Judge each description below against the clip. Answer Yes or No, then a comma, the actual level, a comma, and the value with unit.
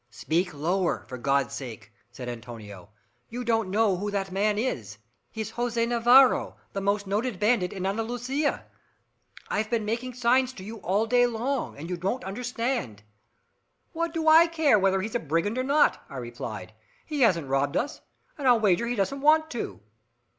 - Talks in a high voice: Yes, high, 215 Hz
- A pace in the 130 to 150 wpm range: No, average, 175 wpm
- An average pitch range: No, wide, 6.6 semitones